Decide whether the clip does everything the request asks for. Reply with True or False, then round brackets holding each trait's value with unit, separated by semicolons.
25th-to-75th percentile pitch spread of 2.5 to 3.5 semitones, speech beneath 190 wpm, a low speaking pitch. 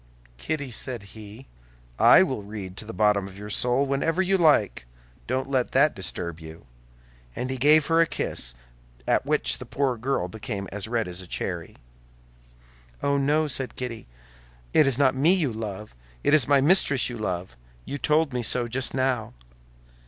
False (5.2 semitones; 175 wpm; 125 Hz)